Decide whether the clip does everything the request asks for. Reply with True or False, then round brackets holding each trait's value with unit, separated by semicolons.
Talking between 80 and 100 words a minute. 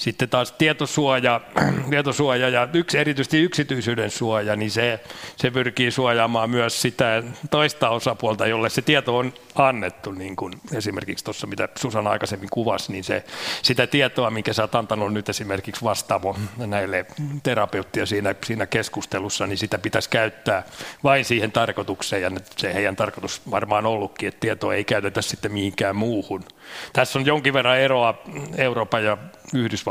False (155 wpm)